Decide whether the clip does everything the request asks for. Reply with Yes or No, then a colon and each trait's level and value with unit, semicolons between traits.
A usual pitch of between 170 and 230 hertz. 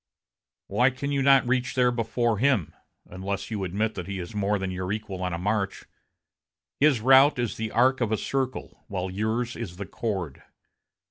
No: low, 110 Hz